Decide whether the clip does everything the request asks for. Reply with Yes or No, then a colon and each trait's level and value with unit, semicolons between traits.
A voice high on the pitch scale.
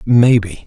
No: low, 110 Hz